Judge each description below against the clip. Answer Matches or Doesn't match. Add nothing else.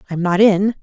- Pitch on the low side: Doesn't match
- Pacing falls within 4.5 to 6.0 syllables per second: Matches